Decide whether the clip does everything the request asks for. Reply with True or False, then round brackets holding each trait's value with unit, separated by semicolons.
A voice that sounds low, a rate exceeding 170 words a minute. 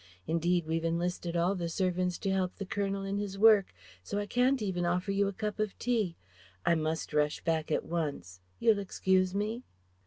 False (185 Hz; 190 wpm)